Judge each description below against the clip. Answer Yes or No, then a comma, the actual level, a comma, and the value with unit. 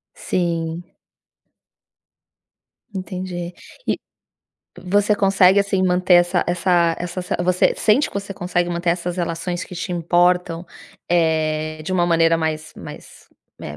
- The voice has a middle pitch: Yes, medium, 175 Hz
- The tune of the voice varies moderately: No, narrow, 1.7 semitones